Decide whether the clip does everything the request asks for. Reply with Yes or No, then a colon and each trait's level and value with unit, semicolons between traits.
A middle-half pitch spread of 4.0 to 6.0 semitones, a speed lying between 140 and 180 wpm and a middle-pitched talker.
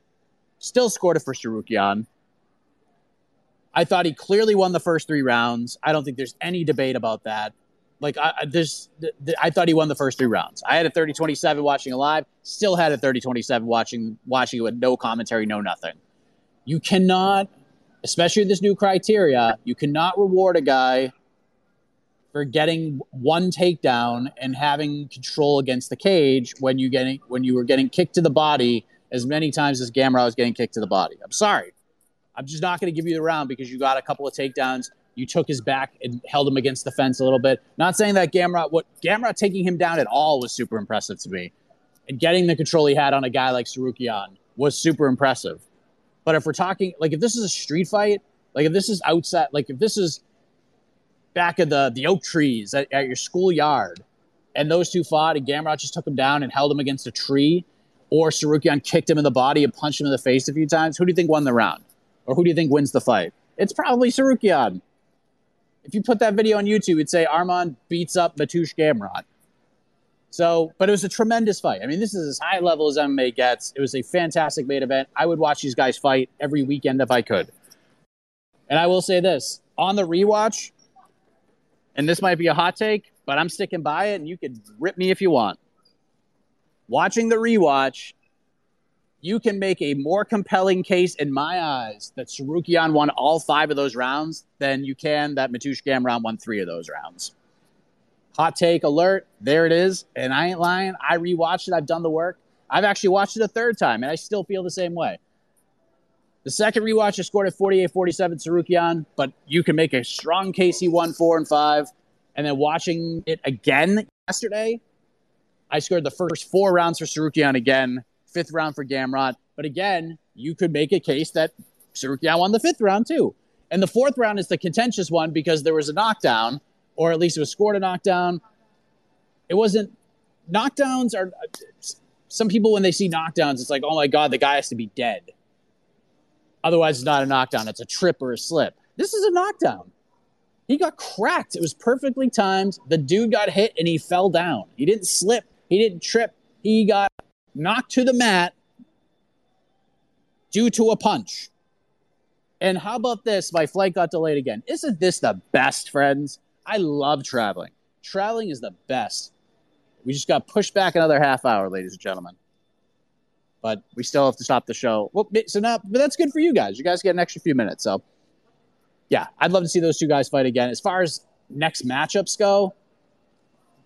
No: wide, 5.5 semitones; fast, 205 wpm; medium, 165 Hz